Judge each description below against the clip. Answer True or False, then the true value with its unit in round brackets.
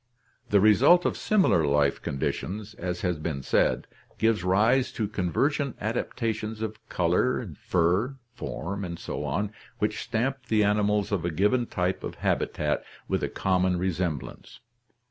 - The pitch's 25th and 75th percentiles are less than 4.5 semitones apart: True (4.1 semitones)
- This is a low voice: True (100 Hz)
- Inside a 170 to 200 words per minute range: False (145 wpm)